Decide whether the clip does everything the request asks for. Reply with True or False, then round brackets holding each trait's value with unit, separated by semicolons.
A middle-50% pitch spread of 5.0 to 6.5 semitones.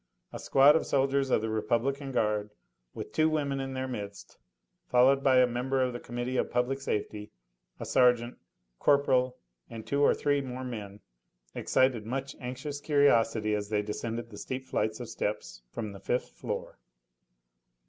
False (3.9 semitones)